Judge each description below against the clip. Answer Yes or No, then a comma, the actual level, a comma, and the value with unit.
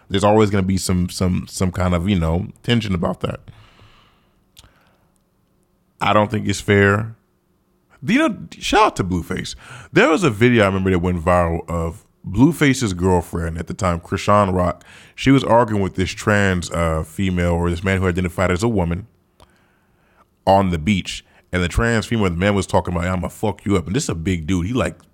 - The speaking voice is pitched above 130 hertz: No, very low, 95 Hz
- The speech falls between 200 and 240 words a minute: Yes, fast, 205 wpm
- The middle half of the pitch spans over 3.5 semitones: No, average, 2.7 semitones